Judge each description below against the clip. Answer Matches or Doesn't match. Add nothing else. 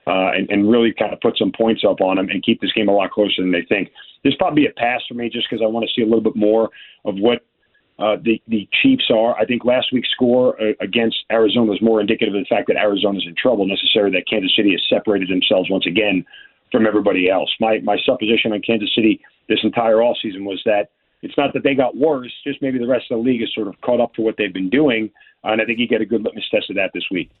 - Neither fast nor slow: Doesn't match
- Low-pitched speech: Matches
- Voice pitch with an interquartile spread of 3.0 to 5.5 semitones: Doesn't match